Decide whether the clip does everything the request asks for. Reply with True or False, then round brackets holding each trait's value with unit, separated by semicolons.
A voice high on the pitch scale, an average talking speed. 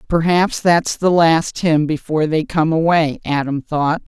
False (160 Hz; 160 wpm)